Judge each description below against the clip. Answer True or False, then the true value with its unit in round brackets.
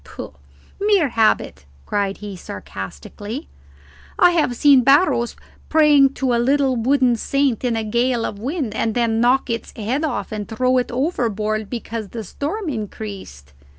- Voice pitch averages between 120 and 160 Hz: False (240 Hz)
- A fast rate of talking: False (150 wpm)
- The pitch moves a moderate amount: True (4.3 semitones)